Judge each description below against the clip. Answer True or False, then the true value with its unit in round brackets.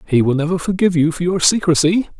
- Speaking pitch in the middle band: True (170 Hz)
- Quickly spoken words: True (220 wpm)